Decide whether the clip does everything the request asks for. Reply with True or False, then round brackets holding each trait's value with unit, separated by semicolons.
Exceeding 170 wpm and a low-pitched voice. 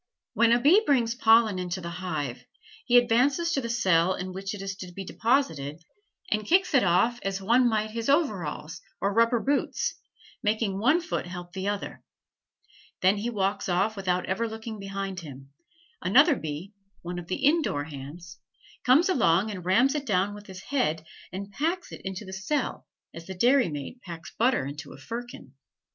False (180 wpm; 200 Hz)